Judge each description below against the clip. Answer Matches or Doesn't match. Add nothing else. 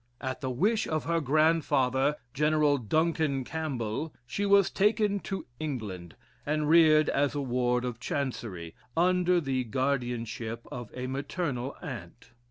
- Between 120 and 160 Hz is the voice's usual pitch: Matches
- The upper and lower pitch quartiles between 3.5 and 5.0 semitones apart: Matches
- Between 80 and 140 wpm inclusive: Matches